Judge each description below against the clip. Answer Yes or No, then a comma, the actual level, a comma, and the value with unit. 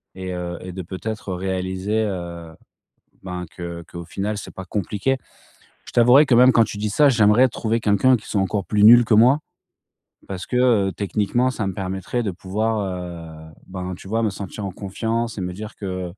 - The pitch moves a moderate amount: Yes, average, 3.4 semitones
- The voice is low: Yes, low, 100 Hz